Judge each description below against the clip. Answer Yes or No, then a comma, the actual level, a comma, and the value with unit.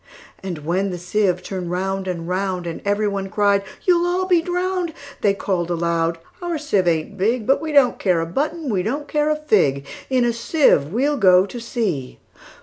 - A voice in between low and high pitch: No, high, 200 Hz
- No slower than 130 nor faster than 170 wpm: No, average, 180 wpm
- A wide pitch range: Yes, wide, 8.1 semitones